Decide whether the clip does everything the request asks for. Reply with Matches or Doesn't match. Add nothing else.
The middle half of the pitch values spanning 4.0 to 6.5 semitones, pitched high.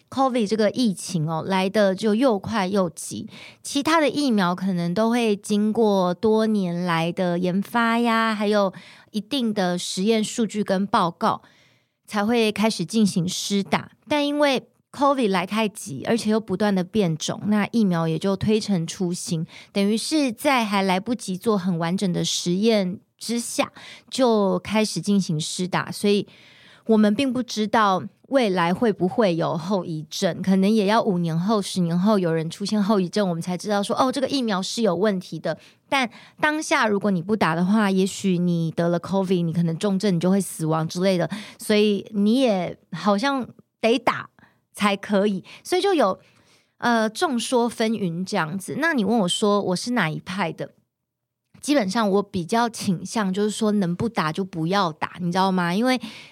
Doesn't match